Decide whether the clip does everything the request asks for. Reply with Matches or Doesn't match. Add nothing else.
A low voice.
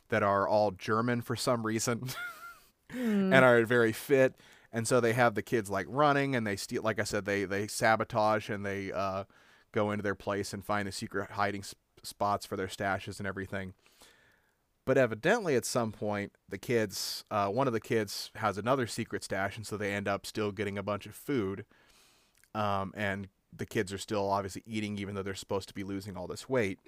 Matches